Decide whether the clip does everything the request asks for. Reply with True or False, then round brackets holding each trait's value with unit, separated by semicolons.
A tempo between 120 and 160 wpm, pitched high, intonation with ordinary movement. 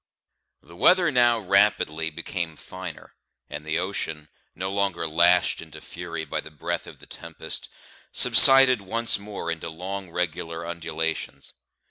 False (135 wpm; 85 Hz; 3.5 semitones)